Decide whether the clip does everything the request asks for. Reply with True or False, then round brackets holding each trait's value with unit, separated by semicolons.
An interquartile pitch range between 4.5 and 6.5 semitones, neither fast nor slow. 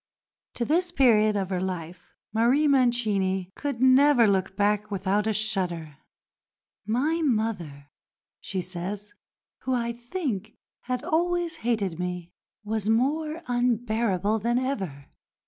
False (5.0 semitones; 120 wpm)